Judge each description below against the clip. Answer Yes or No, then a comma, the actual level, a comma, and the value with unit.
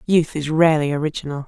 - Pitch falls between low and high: Yes, medium, 155 Hz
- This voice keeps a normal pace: Yes, average, 160 wpm